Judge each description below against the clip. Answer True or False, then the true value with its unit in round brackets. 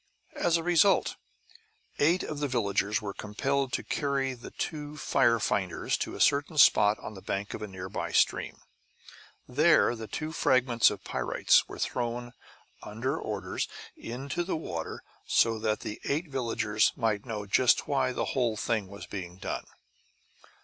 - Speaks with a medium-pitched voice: False (120 Hz)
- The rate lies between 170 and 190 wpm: False (155 wpm)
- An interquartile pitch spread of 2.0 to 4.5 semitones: False (5.2 semitones)